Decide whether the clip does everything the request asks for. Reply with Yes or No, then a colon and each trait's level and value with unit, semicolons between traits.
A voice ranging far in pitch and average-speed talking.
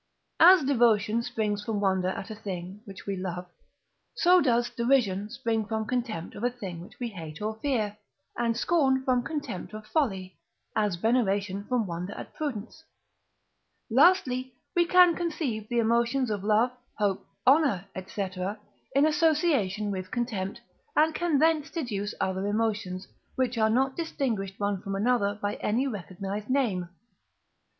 No: average, 4.8 semitones; average, 150 wpm